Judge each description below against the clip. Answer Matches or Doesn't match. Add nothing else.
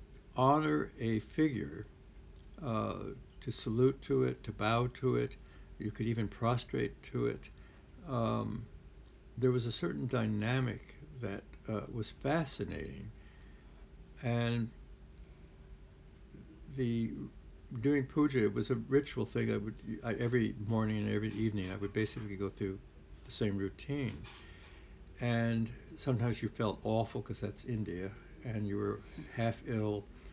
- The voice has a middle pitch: Doesn't match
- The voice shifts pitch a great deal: Doesn't match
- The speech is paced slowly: Matches